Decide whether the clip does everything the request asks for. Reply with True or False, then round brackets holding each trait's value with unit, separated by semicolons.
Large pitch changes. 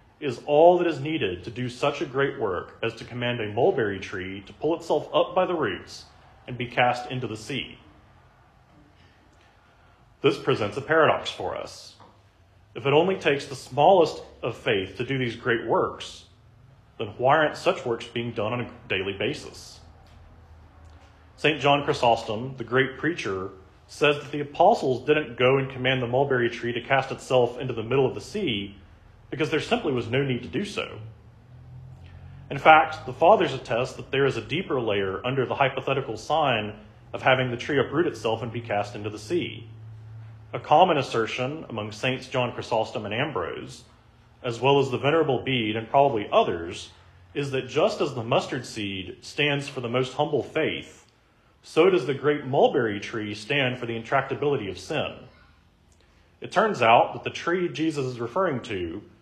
False (4.2 semitones)